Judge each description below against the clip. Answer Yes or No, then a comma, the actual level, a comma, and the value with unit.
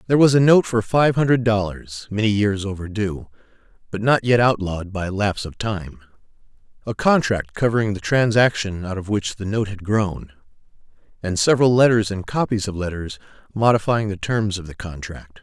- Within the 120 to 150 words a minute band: No, average, 170 wpm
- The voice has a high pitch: No, low, 105 Hz